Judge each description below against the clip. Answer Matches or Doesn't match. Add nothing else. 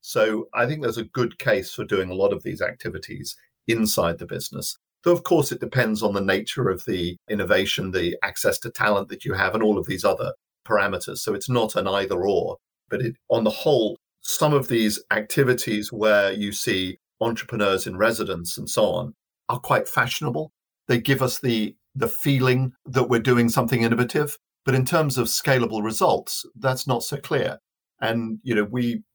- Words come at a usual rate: Matches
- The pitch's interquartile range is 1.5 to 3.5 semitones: Doesn't match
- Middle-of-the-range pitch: Doesn't match